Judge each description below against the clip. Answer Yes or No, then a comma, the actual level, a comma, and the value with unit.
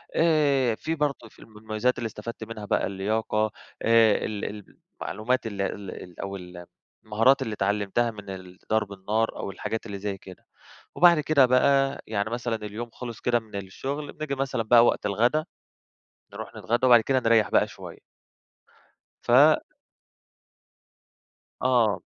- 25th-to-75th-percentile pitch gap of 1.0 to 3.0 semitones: No, average, 3.7 semitones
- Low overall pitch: Yes, low, 110 Hz